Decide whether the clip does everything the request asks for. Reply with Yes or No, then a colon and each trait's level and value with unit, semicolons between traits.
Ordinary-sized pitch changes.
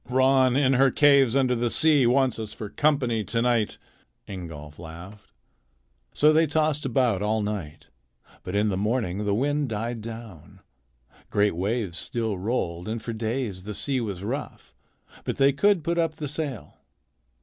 Yes: average, 4.9 semitones